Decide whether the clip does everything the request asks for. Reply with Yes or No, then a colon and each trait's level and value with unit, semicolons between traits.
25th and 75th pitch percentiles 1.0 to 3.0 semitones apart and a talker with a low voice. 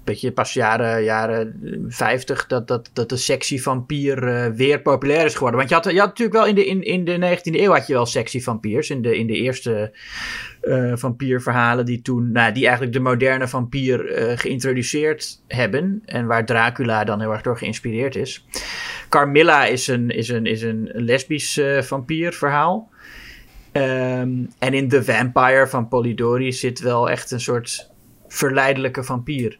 Yes: narrow, 2.4 semitones; low, 125 Hz